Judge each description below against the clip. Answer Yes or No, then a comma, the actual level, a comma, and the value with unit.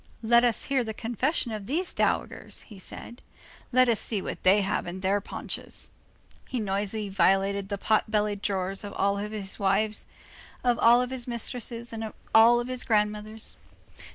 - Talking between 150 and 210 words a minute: Yes, average, 165 wpm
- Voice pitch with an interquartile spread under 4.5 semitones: Yes, average, 3.0 semitones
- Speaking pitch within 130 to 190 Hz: No, high, 215 Hz